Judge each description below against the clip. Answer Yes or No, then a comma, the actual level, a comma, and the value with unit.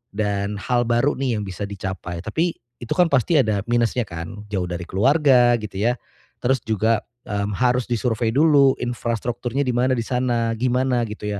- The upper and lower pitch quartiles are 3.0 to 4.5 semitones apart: Yes, average, 3.5 semitones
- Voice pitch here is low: Yes, low, 120 Hz